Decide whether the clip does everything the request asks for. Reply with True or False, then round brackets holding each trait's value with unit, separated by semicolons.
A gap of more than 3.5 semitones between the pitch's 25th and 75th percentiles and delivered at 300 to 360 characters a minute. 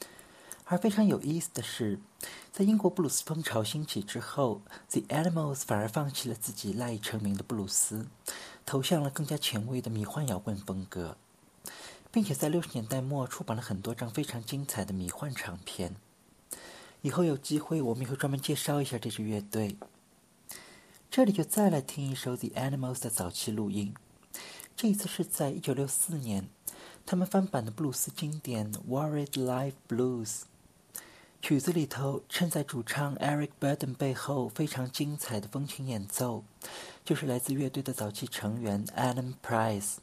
True (5.3 semitones; 315 characters per minute)